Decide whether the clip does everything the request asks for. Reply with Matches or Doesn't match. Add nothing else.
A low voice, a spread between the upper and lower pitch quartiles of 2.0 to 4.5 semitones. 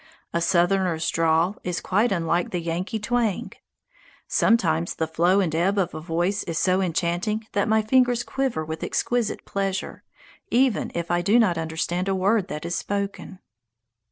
Doesn't match